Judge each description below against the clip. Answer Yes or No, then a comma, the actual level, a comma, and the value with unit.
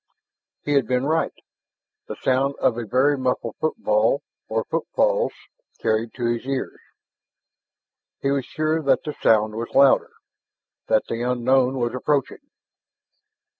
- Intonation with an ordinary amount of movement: Yes, average, 3.3 semitones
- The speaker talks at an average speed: No, slow, 130 wpm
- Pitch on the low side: Yes, low, 130 Hz